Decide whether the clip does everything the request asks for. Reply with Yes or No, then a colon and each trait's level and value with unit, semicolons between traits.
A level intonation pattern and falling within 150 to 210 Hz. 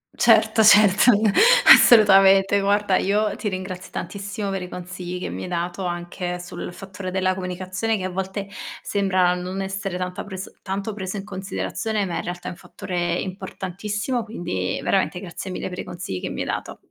Yes: narrow, 1.8 semitones; high, 190 Hz